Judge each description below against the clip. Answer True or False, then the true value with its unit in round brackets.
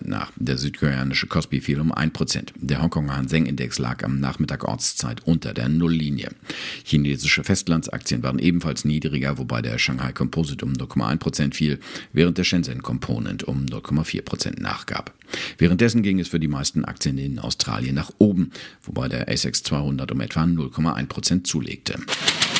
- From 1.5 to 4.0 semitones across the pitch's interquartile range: True (3.3 semitones)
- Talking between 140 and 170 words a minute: True (150 wpm)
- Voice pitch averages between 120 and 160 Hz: False (75 Hz)